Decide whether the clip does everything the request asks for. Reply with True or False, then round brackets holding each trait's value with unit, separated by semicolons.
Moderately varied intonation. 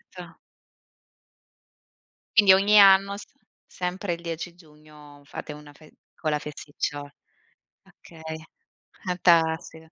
True (3.2 semitones)